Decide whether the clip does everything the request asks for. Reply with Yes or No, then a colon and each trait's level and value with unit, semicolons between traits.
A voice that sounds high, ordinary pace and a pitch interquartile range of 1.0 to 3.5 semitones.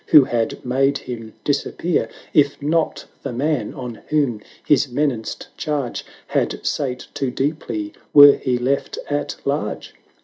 No: low, 135 Hz; average, 145 wpm; average, 3.1 semitones